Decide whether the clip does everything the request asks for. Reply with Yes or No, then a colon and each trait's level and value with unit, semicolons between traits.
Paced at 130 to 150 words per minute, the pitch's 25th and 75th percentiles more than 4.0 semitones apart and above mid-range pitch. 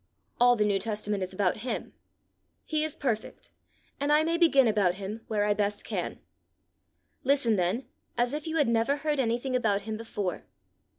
No: average, 175 wpm; average, 5.2 semitones; high, 230 Hz